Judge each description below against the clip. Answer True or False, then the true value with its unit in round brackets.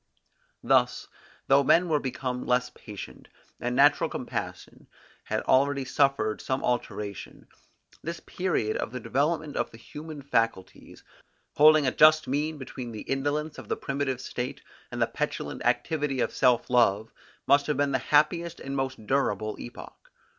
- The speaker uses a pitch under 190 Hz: True (135 Hz)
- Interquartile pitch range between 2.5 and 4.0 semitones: True (3.3 semitones)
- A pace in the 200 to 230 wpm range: False (150 wpm)